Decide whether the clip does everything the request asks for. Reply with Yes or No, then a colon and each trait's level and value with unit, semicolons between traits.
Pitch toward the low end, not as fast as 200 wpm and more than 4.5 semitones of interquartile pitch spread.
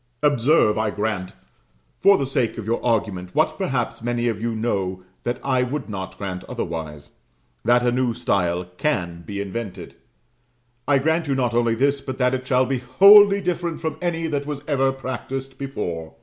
Yes: low, 125 Hz; average, 180 wpm; average, 5.1 semitones